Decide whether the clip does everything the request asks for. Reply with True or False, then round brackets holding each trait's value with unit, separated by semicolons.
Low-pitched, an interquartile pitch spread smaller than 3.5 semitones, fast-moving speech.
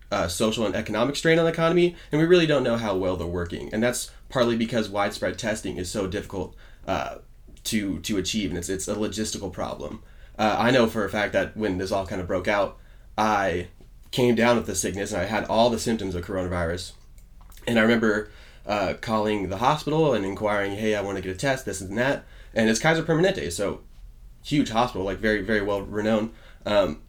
False (105 Hz; 4.0 semitones; 215 wpm)